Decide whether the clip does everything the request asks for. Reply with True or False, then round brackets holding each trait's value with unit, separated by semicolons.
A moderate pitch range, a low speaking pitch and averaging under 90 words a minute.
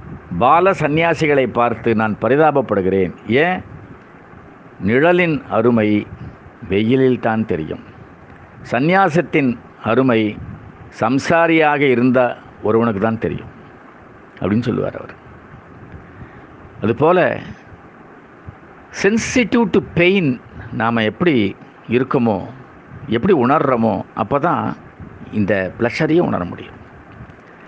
False (6.3 semitones; 125 Hz; 80 wpm)